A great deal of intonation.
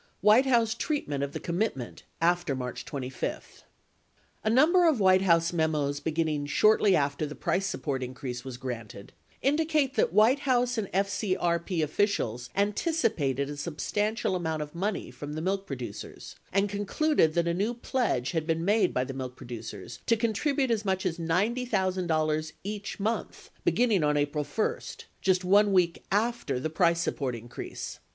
Yes: wide, 6.6 semitones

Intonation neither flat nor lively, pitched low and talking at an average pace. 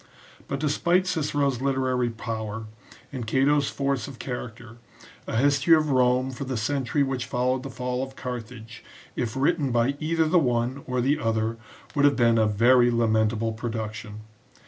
Yes: average, 3.2 semitones; low, 125 Hz; average, 160 wpm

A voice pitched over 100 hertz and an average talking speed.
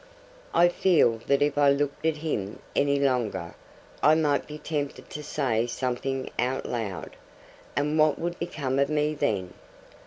Yes: medium, 140 Hz; average, 155 wpm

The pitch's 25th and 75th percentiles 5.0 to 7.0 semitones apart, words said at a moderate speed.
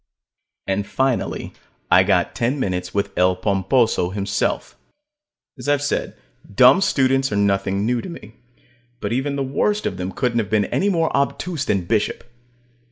Yes: wide, 5.6 semitones; average, 160 wpm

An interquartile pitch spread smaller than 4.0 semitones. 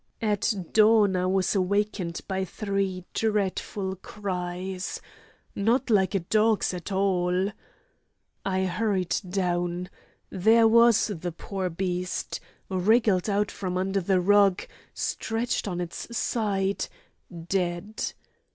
Yes: narrow, 2.5 semitones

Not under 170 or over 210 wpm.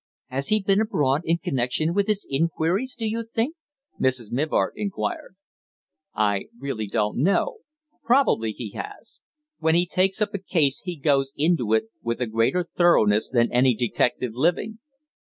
No: average, 160 wpm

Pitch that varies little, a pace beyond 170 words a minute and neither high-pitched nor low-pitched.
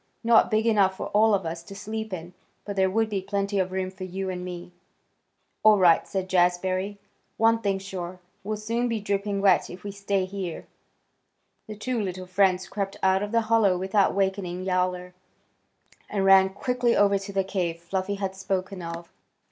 No: narrow, 1.8 semitones; average, 185 wpm; high, 195 Hz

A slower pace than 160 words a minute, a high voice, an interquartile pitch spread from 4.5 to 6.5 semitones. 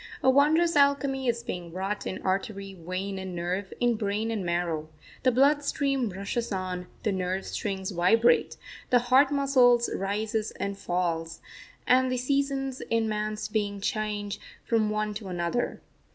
Yes: average, 150 wpm; high, 215 Hz; average, 4.9 semitones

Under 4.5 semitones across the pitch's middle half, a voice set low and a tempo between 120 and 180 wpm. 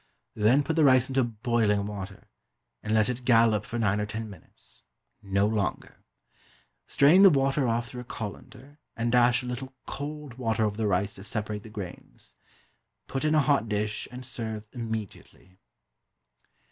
Yes: average, 3.8 semitones; low, 115 Hz; average, 165 wpm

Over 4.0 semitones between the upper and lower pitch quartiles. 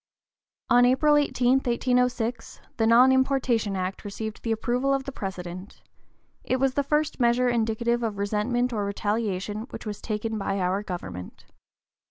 No: average, 3.5 semitones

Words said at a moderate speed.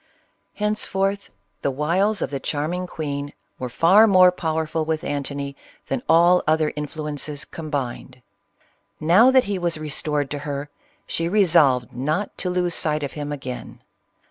Yes: average, 150 wpm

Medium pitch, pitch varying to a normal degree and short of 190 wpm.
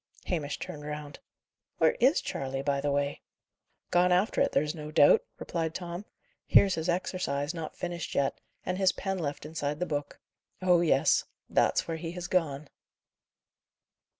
Yes: medium, 160 Hz; average, 3.6 semitones; average, 155 wpm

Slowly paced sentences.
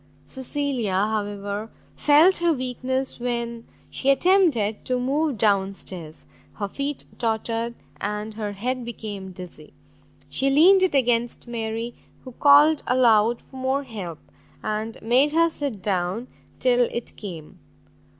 Yes: slow, 130 wpm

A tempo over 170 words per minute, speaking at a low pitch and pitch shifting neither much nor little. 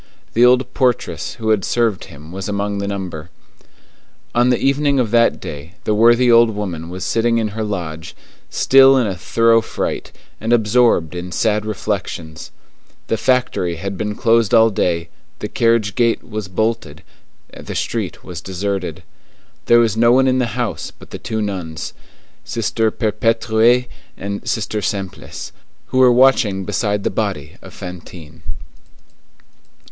No: average, 150 wpm; low, 110 Hz; average, 4.0 semitones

